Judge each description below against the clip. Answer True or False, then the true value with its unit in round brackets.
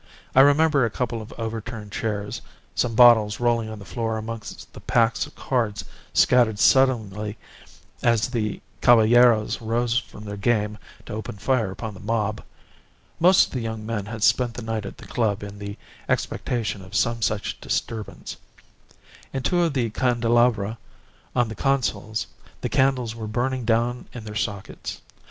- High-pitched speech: False (115 Hz)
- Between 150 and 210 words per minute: True (160 wpm)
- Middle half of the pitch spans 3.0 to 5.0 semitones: False (2.4 semitones)